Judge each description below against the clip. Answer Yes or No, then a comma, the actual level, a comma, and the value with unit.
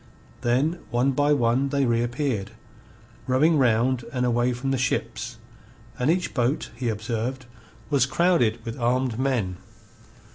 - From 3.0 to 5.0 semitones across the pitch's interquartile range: No, narrow, 2.6 semitones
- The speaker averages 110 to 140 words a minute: Yes, slow, 135 wpm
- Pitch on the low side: Yes, low, 125 Hz